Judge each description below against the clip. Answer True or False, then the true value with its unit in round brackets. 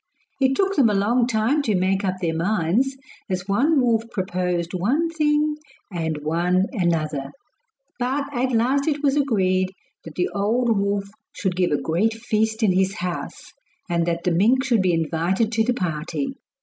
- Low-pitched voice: False (200 Hz)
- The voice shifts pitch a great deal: True (5.9 semitones)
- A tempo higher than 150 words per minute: True (175 wpm)